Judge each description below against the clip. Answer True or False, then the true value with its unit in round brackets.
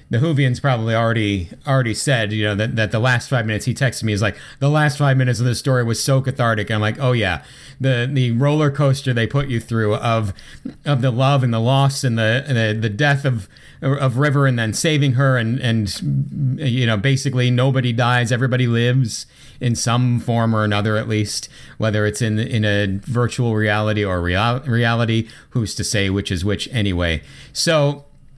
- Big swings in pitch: False (3.6 semitones)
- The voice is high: False (120 Hz)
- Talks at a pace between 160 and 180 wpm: False (205 wpm)